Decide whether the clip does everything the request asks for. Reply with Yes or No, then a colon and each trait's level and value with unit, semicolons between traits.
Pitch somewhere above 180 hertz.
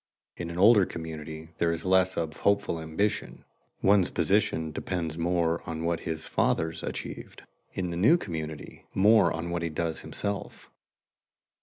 No: very low, 85 Hz